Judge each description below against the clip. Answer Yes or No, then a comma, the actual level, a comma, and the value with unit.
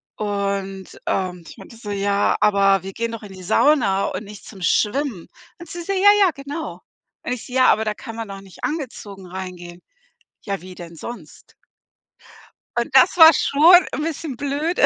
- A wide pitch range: Yes, wide, 6.6 semitones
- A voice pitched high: Yes, high, 210 Hz